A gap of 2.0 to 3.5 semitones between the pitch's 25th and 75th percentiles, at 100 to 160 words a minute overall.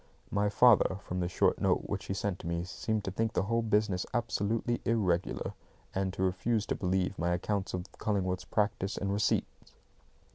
No: average, 2.7 semitones; average, 175 wpm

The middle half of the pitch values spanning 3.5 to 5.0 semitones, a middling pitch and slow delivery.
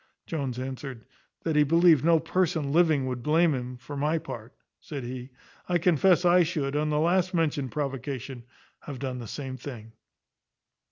No: average, 4.1 semitones; medium, 145 Hz; average, 165 wpm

